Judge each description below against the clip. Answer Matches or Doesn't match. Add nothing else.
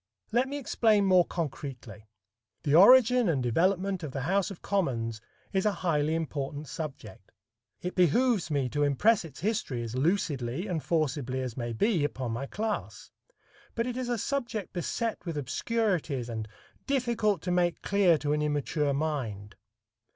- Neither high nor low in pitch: Matches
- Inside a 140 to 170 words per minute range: Matches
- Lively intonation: Matches